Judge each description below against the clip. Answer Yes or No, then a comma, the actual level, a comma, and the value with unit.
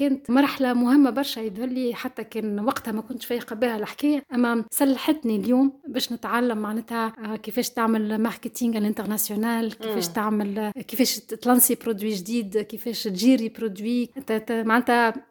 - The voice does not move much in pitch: Yes, narrow, 2.3 semitones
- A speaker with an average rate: No, slow, 130 wpm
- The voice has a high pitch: Yes, high, 230 Hz